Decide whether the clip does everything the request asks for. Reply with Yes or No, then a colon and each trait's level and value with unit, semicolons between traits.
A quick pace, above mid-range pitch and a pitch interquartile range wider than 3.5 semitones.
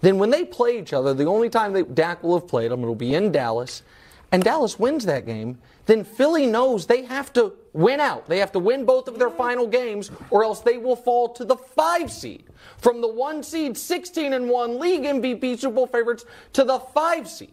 Yes: fast, 225 wpm; high, 245 Hz; average, 4.0 semitones